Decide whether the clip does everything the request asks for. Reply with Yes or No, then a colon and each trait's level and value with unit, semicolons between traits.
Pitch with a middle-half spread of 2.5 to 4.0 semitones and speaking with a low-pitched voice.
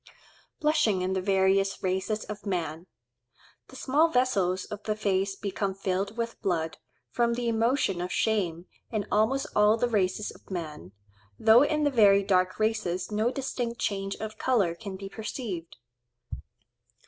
No: average, 3.5 semitones; high, 200 Hz